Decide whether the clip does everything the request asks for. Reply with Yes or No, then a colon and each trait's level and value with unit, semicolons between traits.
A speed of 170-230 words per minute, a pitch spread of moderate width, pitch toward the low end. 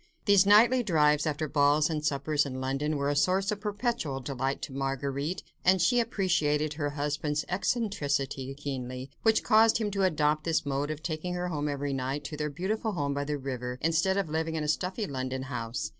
No: average, 195 wpm; average, 4.6 semitones; medium, 150 Hz